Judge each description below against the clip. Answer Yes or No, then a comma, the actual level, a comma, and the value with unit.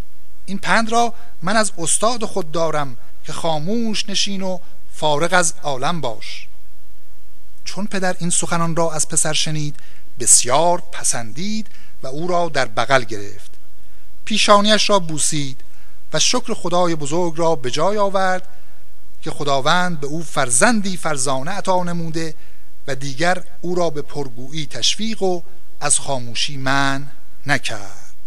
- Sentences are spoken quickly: No, average, 135 wpm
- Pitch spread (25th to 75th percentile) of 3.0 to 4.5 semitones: No, average, 5.0 semitones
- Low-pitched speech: No, medium, 165 Hz